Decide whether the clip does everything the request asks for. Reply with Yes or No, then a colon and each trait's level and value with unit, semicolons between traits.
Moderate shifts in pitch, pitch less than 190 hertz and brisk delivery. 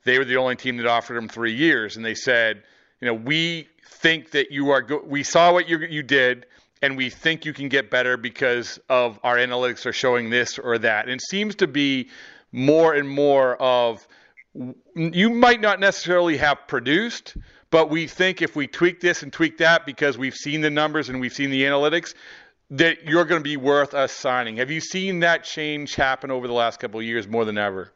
Yes: average, 4.6 semitones; medium, 140 Hz; fast, 215 wpm